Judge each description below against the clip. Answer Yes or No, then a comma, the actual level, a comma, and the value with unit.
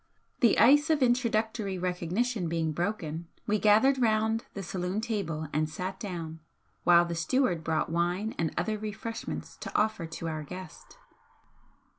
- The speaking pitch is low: No, high, 190 Hz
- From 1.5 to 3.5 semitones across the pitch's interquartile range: No, average, 4.8 semitones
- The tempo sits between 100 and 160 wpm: Yes, average, 145 wpm